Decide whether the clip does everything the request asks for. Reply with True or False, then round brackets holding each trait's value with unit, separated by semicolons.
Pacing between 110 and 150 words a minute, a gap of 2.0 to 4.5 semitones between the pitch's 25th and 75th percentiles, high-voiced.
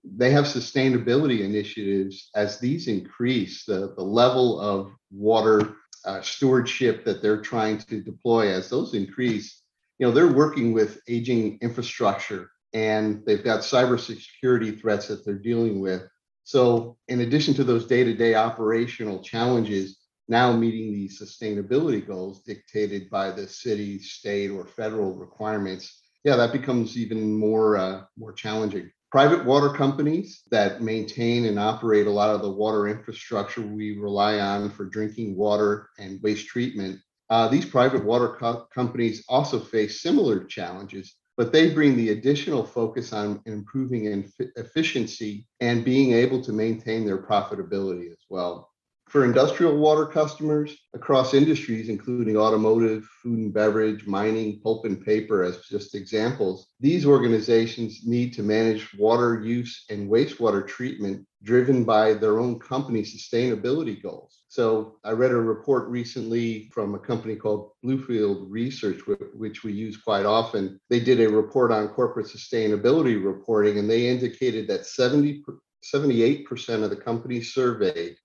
False (145 wpm; 2.8 semitones; 110 Hz)